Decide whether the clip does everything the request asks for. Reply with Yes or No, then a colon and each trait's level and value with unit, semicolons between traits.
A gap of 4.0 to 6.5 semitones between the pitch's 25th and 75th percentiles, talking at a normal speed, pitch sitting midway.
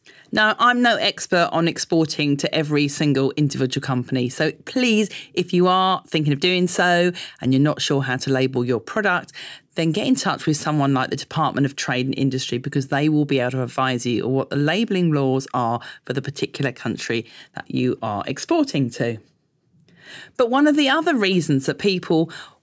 Yes: average, 5.2 semitones; average, 195 wpm; medium, 145 Hz